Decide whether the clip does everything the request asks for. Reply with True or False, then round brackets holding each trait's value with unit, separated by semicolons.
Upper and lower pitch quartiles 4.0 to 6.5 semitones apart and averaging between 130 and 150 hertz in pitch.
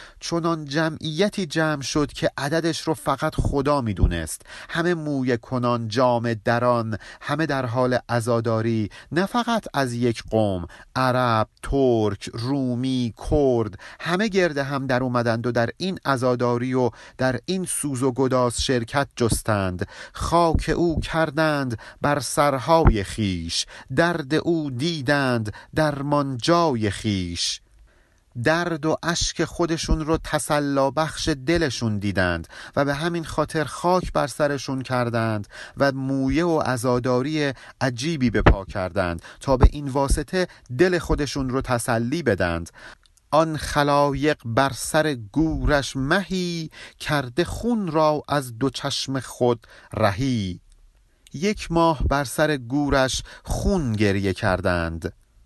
True (5.1 semitones; 135 Hz)